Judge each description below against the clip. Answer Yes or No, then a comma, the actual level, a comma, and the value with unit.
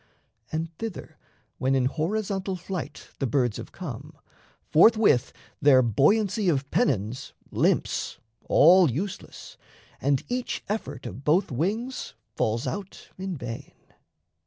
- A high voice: No, medium, 160 Hz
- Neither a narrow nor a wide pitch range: No, wide, 6.8 semitones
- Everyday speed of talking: No, slow, 115 wpm